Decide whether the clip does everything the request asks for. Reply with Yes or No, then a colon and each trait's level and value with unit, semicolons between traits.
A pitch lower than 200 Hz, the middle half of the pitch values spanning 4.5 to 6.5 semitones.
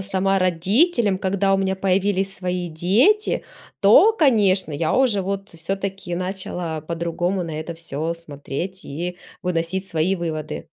No: medium, 185 Hz; average, 2.8 semitones